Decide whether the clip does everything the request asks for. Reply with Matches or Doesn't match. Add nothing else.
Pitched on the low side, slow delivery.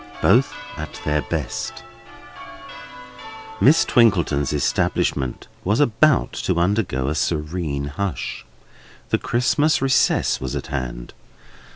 Matches